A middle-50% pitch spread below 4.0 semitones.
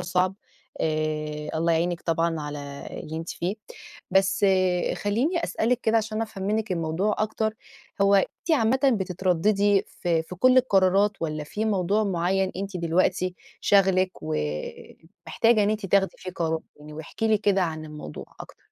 No: average, 4.3 semitones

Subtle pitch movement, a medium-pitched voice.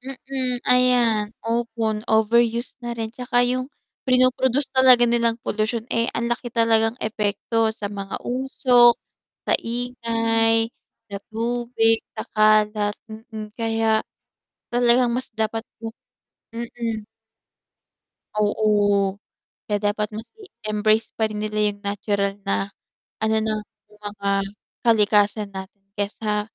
No: narrow, 2.1 semitones; high, 225 Hz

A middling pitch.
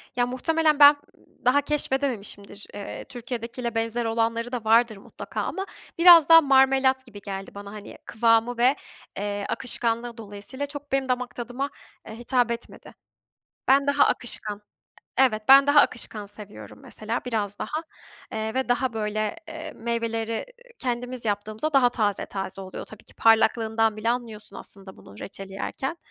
No: high, 235 Hz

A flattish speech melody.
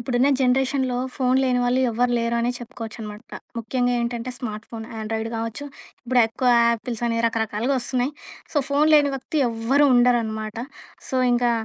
Yes: narrow, 2.1 semitones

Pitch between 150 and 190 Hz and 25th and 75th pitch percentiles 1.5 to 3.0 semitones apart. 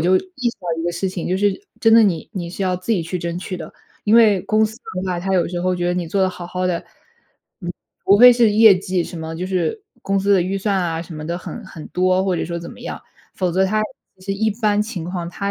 Yes: medium, 185 Hz; narrow, 2.6 semitones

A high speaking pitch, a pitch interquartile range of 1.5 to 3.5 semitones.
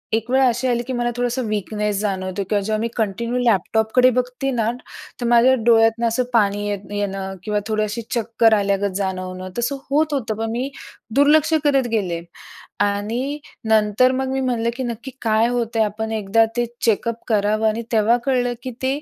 Yes: high, 225 Hz; average, 2.9 semitones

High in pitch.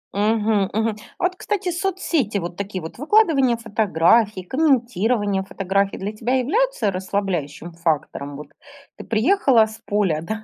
Yes: high, 215 Hz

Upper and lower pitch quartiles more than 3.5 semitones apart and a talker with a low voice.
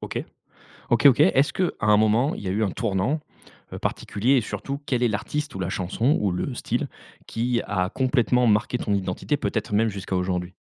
Yes: average, 4.7 semitones; low, 110 Hz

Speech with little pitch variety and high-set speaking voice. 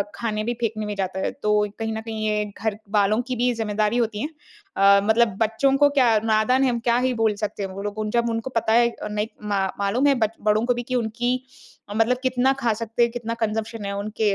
Yes: narrow, 2.3 semitones; high, 225 Hz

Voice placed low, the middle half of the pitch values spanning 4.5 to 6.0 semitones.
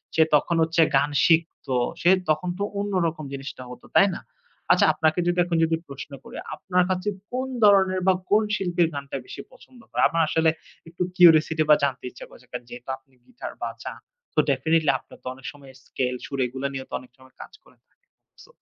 No: medium, 160 Hz; average, 4.8 semitones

